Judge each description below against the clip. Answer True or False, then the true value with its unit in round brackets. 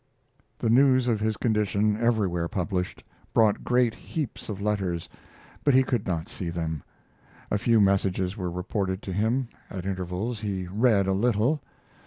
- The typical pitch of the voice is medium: False (105 Hz)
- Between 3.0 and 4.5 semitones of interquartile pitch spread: True (3.8 semitones)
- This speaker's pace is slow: False (155 wpm)